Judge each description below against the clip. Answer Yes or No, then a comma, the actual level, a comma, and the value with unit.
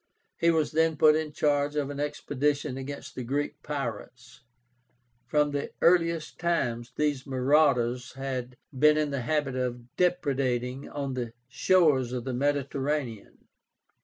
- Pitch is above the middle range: No, medium, 140 Hz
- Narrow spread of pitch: No, average, 3.0 semitones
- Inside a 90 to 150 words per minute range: Yes, slow, 135 wpm